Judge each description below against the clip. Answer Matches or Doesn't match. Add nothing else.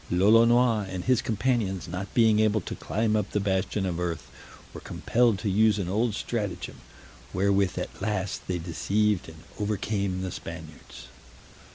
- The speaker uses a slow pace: Doesn't match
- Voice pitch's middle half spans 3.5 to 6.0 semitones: Doesn't match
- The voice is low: Matches